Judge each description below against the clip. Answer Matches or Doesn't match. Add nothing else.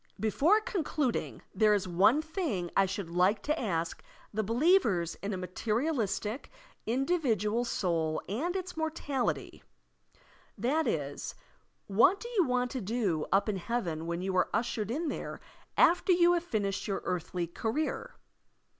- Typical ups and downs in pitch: Doesn't match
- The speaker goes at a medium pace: Matches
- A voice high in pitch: Matches